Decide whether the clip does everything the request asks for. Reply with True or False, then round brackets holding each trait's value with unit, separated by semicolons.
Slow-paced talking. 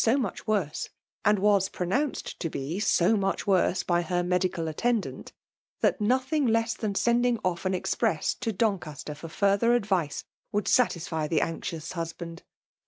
False (155 wpm)